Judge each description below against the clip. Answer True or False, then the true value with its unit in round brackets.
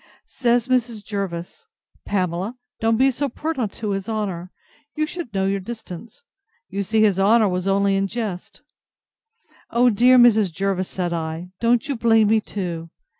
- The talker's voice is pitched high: True (210 Hz)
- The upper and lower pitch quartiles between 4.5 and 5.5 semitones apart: False (3.9 semitones)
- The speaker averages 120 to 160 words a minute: True (155 wpm)